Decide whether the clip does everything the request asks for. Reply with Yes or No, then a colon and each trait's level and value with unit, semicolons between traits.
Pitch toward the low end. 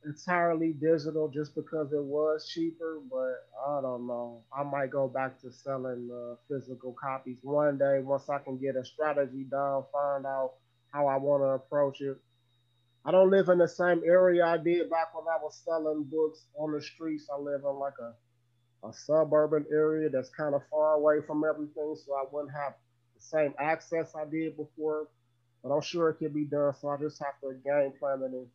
No: medium, 145 Hz